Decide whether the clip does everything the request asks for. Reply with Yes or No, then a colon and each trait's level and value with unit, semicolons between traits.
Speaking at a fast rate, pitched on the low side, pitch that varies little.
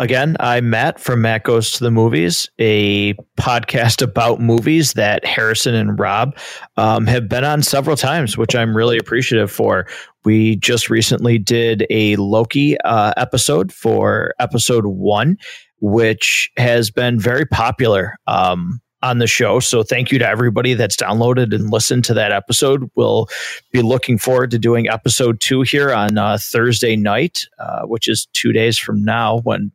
No: average, 165 wpm; low, 115 Hz; narrow, 2.3 semitones